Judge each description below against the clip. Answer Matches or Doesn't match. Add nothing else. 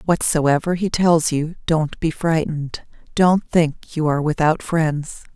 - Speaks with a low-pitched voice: Doesn't match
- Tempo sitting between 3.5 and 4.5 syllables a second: Matches